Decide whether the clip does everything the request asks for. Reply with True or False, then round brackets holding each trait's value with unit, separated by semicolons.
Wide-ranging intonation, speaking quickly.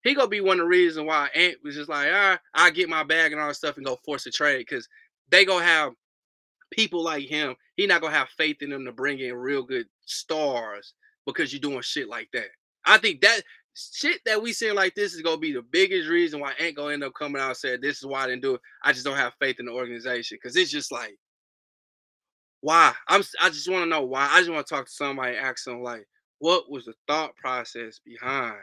True (8.0 semitones; 255 wpm)